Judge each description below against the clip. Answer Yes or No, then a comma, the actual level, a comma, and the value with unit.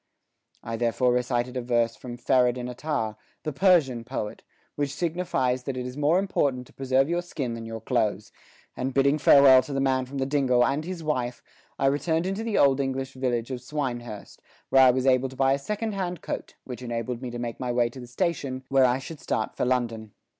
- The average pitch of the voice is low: Yes, low, 130 Hz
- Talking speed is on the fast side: Yes, fast, 210 wpm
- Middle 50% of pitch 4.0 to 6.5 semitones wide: No, narrow, 2.6 semitones